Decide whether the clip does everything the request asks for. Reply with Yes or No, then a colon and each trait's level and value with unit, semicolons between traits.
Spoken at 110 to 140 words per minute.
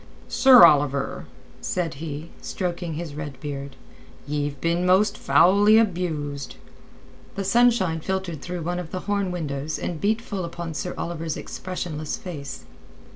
Yes: slow, 135 wpm